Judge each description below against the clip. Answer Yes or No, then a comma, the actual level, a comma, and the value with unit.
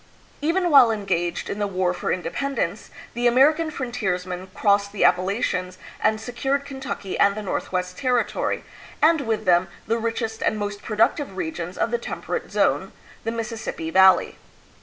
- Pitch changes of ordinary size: Yes, average, 4.9 semitones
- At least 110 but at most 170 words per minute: Yes, average, 155 wpm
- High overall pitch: Yes, high, 215 Hz